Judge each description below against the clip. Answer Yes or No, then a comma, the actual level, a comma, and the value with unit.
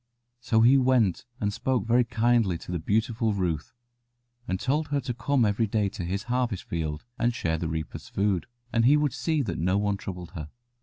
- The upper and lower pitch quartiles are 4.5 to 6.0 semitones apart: Yes, average, 5.3 semitones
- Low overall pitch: Yes, low, 110 Hz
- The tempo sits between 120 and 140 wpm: No, average, 200 wpm